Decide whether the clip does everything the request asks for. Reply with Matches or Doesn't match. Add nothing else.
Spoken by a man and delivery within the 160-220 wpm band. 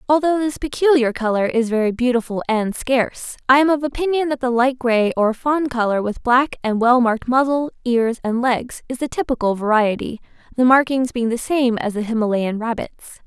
Doesn't match